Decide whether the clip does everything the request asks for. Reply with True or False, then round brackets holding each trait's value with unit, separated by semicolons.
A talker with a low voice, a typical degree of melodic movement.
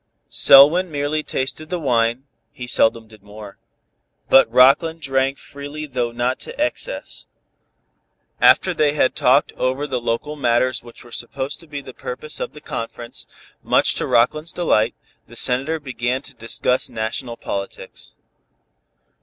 True (130 Hz; 4.1 semitones)